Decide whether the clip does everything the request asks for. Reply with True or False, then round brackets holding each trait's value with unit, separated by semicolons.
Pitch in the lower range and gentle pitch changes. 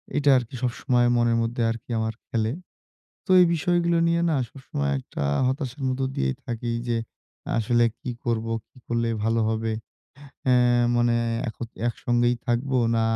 True (120 Hz; 2.3 semitones)